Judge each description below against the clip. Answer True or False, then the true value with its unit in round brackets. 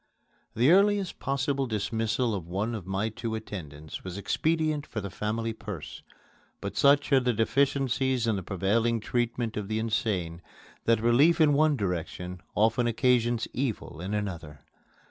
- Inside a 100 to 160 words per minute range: True (150 wpm)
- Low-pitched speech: True (115 Hz)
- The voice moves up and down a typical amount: True (4.8 semitones)